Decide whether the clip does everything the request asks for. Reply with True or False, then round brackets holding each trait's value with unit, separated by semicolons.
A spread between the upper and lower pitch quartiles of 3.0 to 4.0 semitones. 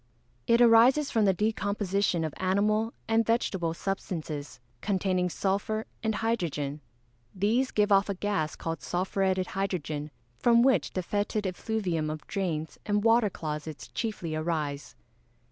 False (4.9 semitones)